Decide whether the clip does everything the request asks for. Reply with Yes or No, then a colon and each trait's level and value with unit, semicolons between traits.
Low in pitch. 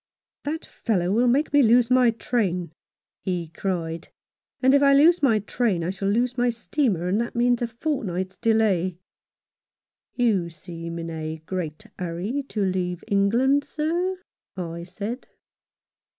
No: high, 210 Hz